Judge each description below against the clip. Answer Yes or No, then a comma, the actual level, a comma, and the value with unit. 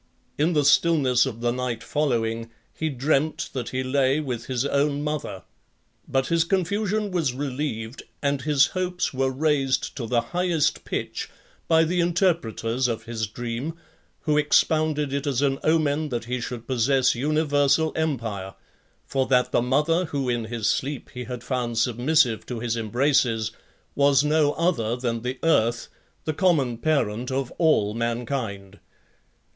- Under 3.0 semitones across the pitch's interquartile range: No, average, 4.3 semitones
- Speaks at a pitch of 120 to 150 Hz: Yes, low, 135 Hz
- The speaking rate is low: No, average, 155 wpm